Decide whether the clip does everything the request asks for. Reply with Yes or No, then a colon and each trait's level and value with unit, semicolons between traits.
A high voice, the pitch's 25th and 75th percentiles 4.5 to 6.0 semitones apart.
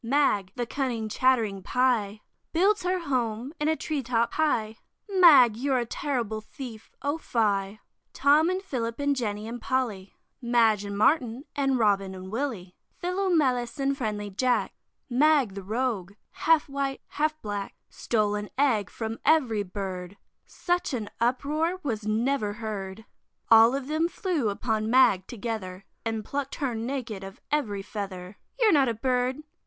Yes: high, 240 Hz; average, 5.0 semitones